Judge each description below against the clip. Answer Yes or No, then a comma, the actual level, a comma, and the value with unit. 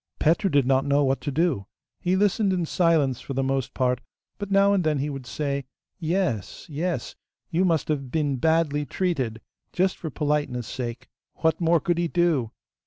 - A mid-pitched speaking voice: Yes, medium, 150 Hz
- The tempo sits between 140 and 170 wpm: No, average, 180 wpm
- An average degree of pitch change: Yes, average, 4.3 semitones